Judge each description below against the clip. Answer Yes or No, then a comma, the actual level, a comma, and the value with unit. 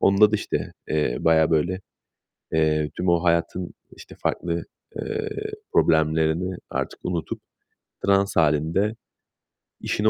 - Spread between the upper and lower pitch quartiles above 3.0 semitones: Yes, average, 3.6 semitones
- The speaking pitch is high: No, very low, 85 Hz